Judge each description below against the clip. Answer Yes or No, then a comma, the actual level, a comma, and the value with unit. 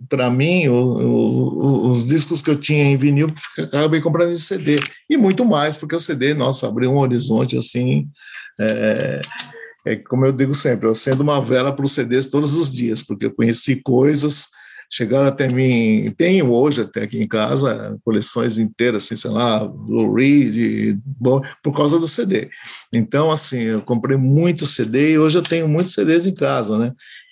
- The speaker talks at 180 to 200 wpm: Yes, fast, 185 wpm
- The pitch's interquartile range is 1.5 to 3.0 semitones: No, average, 3.9 semitones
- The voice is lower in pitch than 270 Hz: Yes, low, 135 Hz